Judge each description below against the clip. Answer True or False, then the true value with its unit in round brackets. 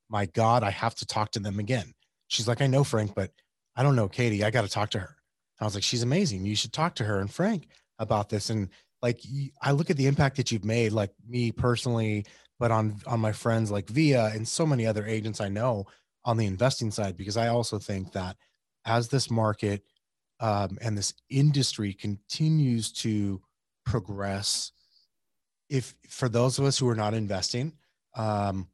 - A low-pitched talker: True (115 Hz)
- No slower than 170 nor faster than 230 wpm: True (200 wpm)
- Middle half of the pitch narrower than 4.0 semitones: True (3.3 semitones)